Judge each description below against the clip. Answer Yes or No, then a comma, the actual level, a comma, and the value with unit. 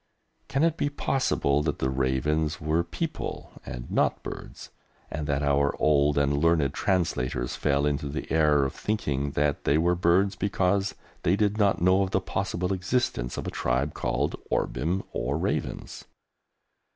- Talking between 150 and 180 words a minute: Yes, average, 160 wpm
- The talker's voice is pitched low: Yes, very low, 75 Hz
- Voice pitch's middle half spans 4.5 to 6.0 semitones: Yes, average, 4.9 semitones